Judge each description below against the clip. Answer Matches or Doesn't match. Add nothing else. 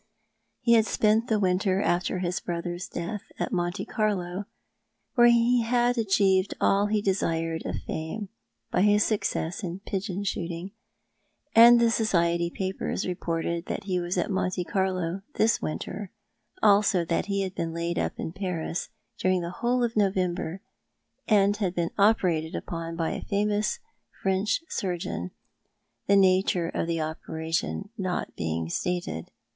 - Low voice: Doesn't match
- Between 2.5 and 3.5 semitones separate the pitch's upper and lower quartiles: Matches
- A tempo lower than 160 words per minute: Matches